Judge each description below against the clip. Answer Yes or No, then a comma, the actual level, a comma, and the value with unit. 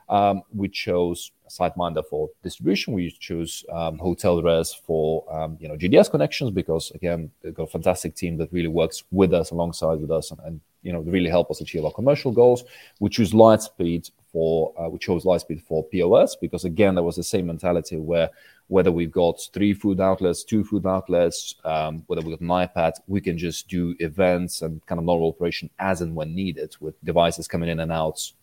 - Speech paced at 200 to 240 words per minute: Yes, fast, 205 wpm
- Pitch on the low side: Yes, very low, 85 Hz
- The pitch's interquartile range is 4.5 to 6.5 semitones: No, narrow, 2.5 semitones